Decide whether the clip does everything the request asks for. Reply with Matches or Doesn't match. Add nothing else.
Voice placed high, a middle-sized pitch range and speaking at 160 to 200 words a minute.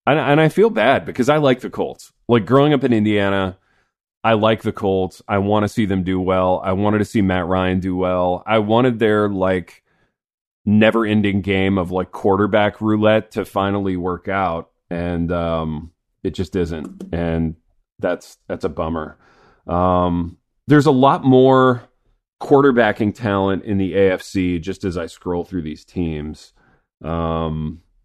Doesn't match